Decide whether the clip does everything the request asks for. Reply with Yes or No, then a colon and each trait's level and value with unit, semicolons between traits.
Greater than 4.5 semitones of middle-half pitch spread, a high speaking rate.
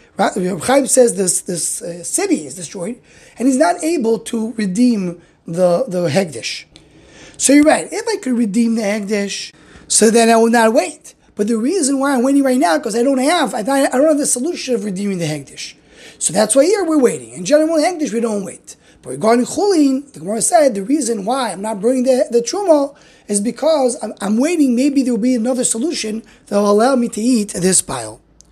Yes: average, 5.2 semitones; fast, 210 wpm